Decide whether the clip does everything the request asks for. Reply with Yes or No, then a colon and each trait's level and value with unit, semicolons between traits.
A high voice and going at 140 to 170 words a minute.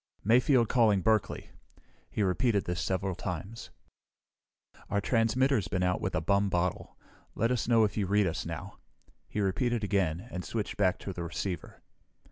No: low, 100 Hz; average, 160 wpm